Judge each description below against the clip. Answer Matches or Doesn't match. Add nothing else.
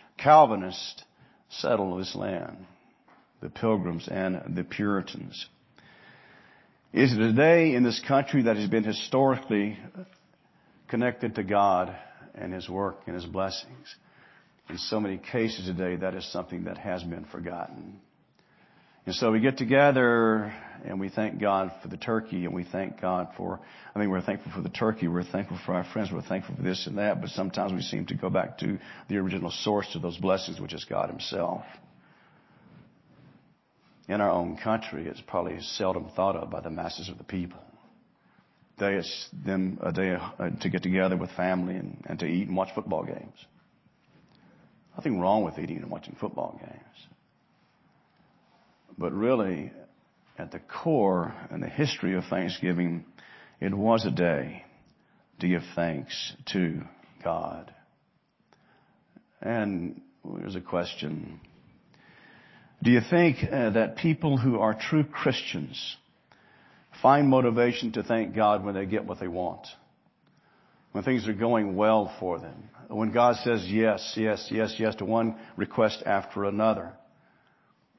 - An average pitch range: Matches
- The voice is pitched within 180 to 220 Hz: Doesn't match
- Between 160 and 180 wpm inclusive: Doesn't match